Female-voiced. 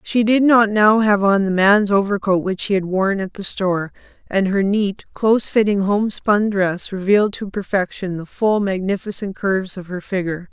Yes: female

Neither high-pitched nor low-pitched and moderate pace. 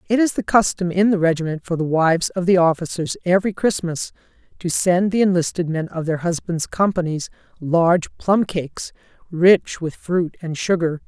Yes: medium, 175 Hz; average, 175 wpm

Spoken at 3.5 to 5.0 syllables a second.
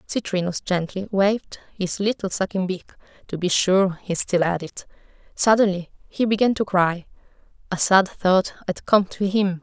Yes: 4.6 syllables/s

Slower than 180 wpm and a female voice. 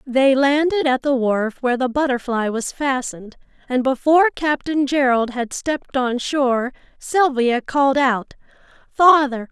Yes: average, 140 wpm; female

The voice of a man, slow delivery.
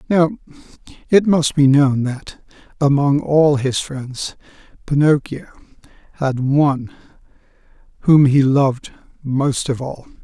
Yes: male; slow, 110 wpm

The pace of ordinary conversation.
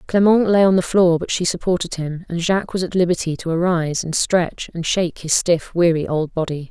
No: fast, 225 wpm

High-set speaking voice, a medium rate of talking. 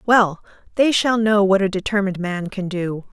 Yes: high, 200 Hz; average, 190 wpm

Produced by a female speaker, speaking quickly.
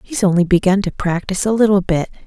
Yes: female; fast, 210 wpm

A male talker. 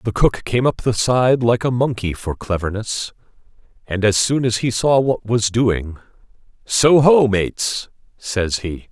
Yes: male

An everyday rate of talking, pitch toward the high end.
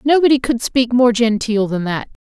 Yes: average, 185 wpm; high, 235 Hz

